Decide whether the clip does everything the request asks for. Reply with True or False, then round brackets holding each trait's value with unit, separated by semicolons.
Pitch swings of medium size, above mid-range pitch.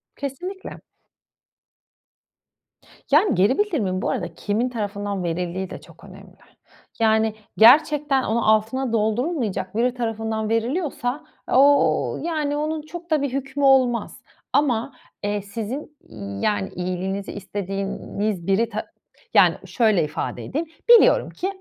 False (5.9 semitones; 230 Hz)